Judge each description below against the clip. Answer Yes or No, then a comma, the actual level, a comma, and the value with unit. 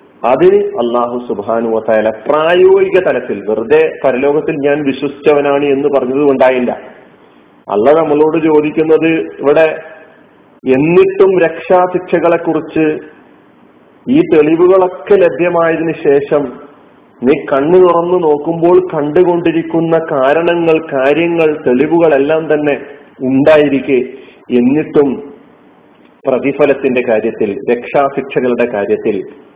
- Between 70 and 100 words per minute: Yes, average, 80 wpm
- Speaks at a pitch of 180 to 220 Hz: No, medium, 155 Hz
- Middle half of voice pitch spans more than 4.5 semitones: No, average, 3.9 semitones